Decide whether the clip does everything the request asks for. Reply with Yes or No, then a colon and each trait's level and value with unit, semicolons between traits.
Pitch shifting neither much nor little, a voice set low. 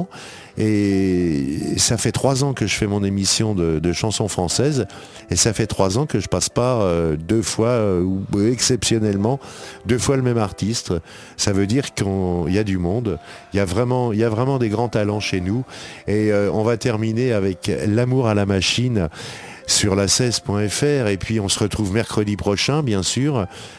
Yes: average, 3.8 semitones; low, 105 Hz